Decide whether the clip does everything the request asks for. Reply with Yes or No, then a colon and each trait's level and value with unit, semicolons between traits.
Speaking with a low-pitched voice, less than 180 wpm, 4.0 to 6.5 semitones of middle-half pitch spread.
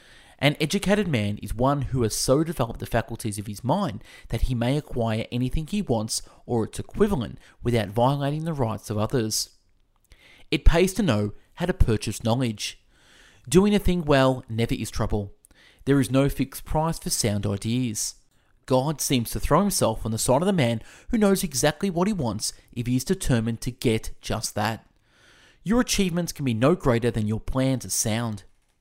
No: low, 120 Hz; average, 185 wpm; average, 5.2 semitones